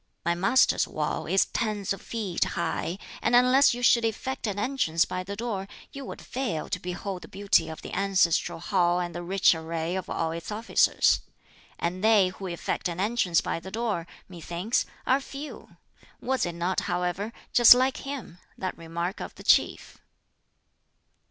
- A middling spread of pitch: Yes, average, 4.9 semitones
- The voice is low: No, high, 190 Hz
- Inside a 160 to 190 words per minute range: Yes, average, 170 wpm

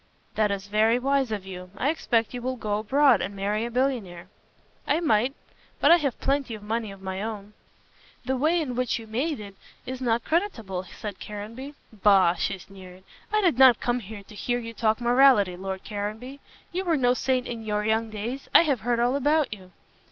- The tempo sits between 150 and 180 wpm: No, fast, 205 wpm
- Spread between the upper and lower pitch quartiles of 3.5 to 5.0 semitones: Yes, average, 4.3 semitones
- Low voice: No, high, 230 Hz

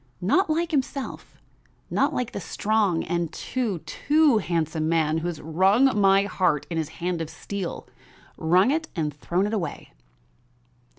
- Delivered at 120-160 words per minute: Yes, average, 155 wpm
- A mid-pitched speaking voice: Yes, medium, 180 Hz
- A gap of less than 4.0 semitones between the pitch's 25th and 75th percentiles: No, average, 5.3 semitones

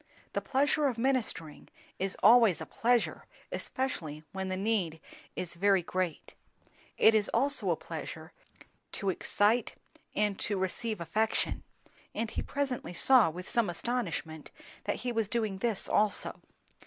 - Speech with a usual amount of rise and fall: Yes, average, 4.5 semitones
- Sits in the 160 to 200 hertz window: No, high, 210 Hz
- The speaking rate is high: No, average, 140 wpm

